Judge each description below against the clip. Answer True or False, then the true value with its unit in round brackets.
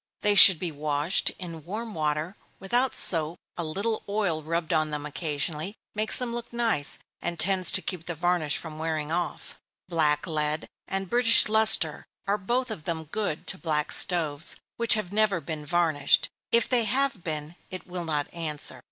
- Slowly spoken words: False (175 wpm)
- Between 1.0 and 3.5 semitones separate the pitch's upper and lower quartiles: False (4.8 semitones)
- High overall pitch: False (170 Hz)